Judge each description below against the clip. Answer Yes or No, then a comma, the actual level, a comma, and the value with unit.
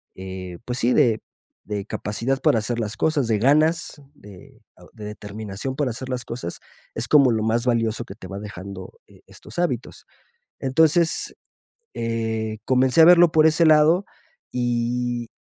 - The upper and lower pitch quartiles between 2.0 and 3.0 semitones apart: No, average, 4.6 semitones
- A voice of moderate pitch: No, low, 120 Hz